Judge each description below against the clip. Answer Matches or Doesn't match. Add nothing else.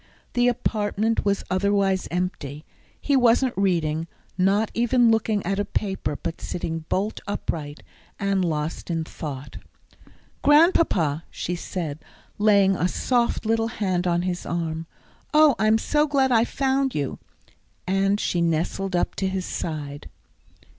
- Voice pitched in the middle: Doesn't match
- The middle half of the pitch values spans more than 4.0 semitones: Matches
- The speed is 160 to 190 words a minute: Doesn't match